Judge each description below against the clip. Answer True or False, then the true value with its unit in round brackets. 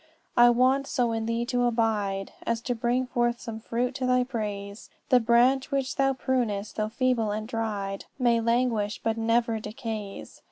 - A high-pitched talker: True (235 Hz)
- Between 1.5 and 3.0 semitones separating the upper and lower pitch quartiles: True (2.4 semitones)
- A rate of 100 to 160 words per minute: False (170 wpm)